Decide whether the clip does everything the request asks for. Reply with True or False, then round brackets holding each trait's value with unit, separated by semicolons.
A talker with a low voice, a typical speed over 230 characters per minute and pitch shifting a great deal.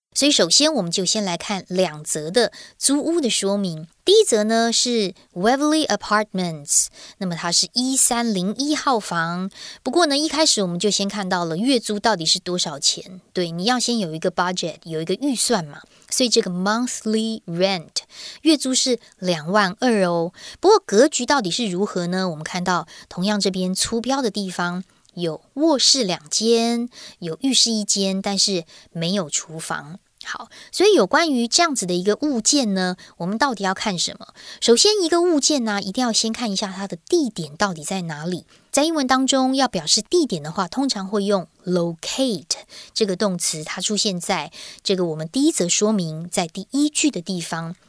False (205 Hz; 305 characters per minute; 5.7 semitones)